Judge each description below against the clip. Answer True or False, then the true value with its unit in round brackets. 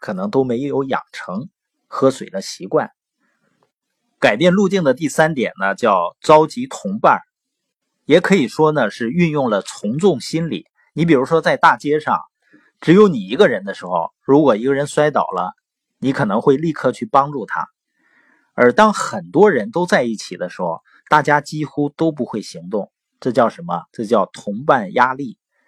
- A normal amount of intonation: True (4.5 semitones)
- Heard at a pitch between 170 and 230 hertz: False (155 Hz)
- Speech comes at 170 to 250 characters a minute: True (245 characters per minute)